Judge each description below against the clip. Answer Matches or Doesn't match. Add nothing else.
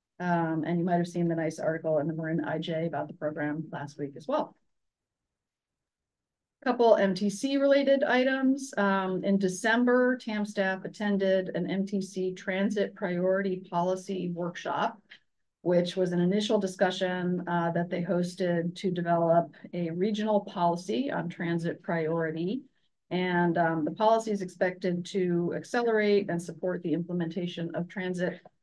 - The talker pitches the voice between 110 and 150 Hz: Doesn't match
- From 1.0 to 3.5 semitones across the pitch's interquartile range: Matches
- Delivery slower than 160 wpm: Matches